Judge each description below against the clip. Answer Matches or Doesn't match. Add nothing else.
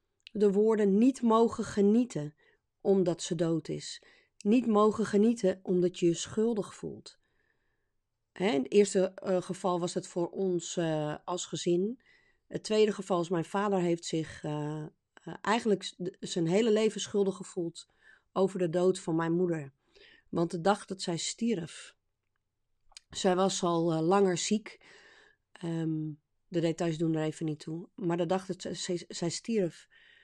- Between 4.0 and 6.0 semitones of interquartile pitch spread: Doesn't match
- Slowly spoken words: Doesn't match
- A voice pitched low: Doesn't match